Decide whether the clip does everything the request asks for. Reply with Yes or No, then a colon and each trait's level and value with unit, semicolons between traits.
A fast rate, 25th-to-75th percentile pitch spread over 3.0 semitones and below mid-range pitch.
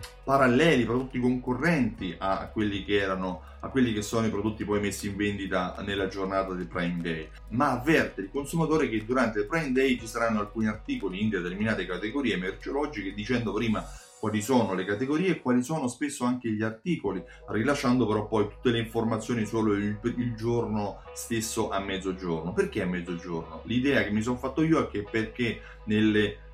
Yes: fast, 175 wpm; average, 3.9 semitones; low, 110 Hz